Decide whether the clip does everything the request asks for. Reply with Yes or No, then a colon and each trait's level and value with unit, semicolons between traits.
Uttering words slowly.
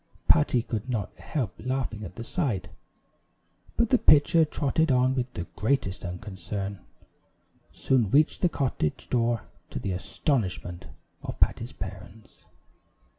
Yes: slow, 125 wpm